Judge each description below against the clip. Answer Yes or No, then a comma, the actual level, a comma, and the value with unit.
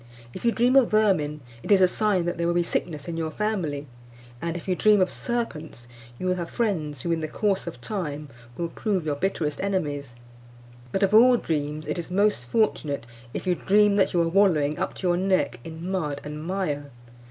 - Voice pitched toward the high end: No, medium, 175 Hz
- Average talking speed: No, fast, 210 wpm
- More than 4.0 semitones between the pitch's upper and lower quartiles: Yes, average, 4.7 semitones